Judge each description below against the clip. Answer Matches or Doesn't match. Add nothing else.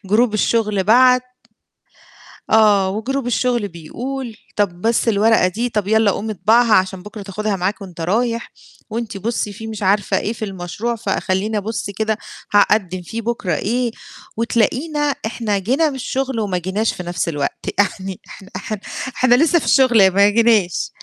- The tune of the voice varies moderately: Matches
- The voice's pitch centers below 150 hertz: Doesn't match